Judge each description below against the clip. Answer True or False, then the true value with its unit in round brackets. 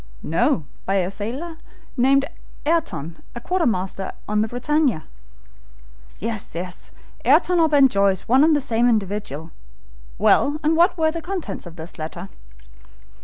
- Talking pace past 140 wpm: False (135 wpm)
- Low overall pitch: False (235 Hz)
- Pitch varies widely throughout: True (8.1 semitones)